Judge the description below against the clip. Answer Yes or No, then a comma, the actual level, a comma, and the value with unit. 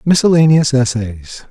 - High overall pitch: No, low, 135 Hz